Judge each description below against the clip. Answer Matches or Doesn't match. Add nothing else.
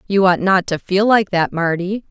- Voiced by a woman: Matches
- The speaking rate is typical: Doesn't match